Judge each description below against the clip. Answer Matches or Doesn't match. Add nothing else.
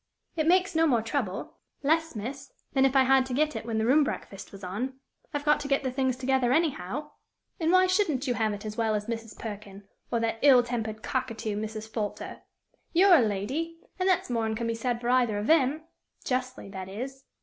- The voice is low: Doesn't match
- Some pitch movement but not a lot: Matches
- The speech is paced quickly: Matches